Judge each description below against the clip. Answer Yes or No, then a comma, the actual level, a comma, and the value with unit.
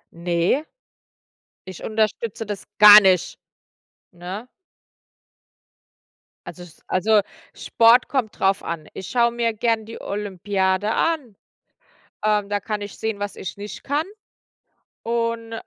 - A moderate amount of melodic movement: Yes, average, 3.2 semitones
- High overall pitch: Yes, high, 210 Hz